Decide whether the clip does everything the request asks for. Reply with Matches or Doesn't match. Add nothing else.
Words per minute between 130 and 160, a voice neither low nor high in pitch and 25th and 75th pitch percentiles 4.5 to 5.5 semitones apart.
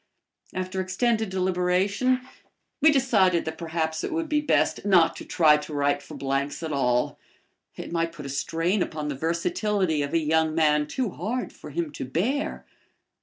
Doesn't match